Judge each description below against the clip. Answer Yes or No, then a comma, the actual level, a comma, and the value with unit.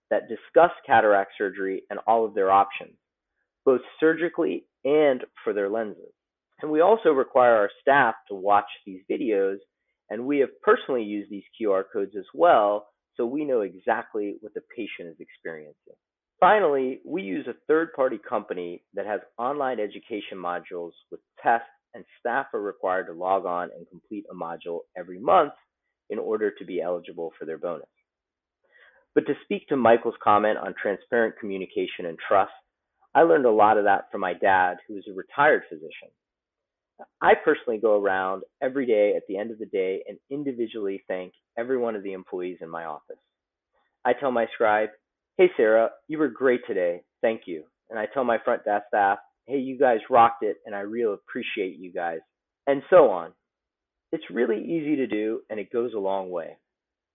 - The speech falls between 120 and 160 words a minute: No, average, 180 wpm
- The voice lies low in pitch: Yes, low, 120 Hz